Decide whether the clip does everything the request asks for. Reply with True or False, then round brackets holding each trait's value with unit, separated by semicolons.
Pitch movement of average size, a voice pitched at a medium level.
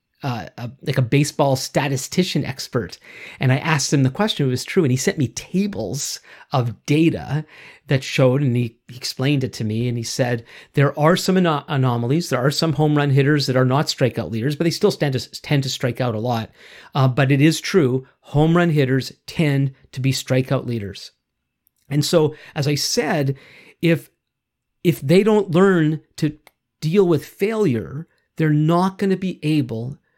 True (3.8 semitones; 145 Hz)